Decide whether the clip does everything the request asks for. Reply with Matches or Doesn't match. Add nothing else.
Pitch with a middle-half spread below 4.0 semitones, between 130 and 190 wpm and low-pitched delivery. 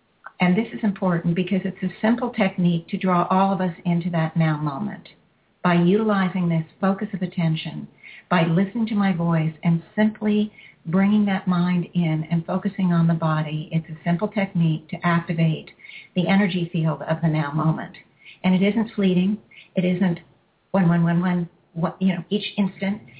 Doesn't match